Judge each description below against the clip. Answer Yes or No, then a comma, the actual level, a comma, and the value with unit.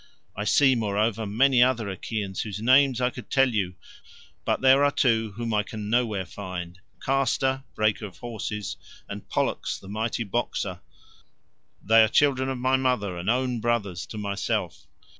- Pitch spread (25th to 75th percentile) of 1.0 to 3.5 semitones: No, average, 4.0 semitones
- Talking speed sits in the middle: Yes, average, 160 wpm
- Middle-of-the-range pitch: No, low, 115 Hz